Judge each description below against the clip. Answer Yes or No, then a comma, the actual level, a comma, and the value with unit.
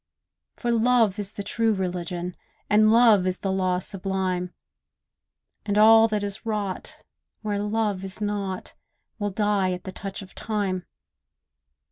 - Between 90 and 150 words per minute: Yes, average, 140 wpm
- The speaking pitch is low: No, high, 200 Hz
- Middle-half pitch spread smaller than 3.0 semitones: Yes, narrow, 2.5 semitones